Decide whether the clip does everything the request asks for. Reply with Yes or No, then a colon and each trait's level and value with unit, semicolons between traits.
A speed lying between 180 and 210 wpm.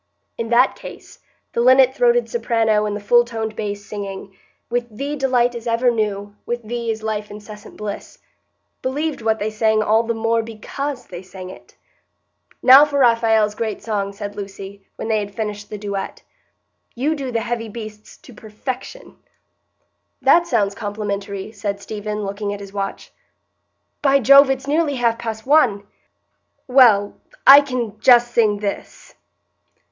No: average, 155 wpm